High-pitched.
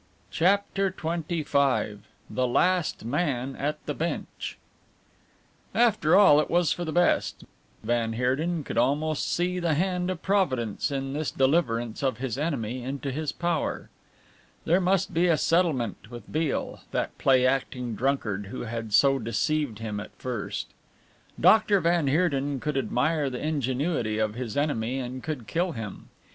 No: medium, 140 Hz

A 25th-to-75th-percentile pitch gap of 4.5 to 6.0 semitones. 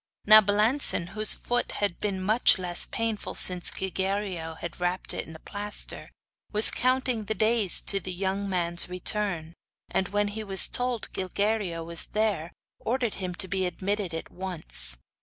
No: average, 3.2 semitones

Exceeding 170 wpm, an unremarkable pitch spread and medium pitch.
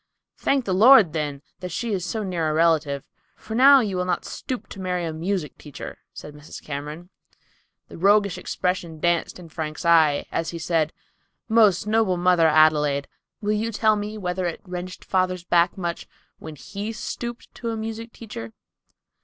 Yes: average, 180 wpm; average, 4.8 semitones; medium, 180 Hz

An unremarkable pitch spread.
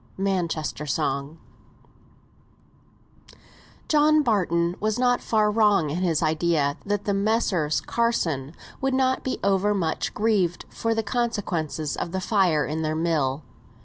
No: wide, 5.7 semitones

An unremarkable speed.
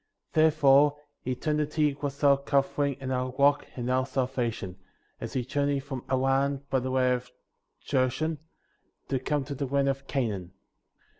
Yes: average, 150 wpm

